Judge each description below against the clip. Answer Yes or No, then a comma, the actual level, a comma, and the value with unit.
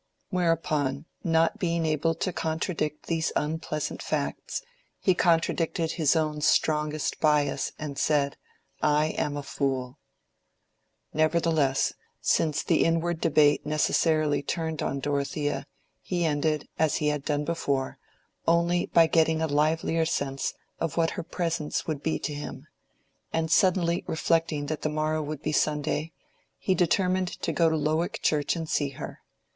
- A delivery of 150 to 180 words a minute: No, average, 140 wpm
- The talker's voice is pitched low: No, medium, 155 Hz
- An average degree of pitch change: No, narrow, 1.9 semitones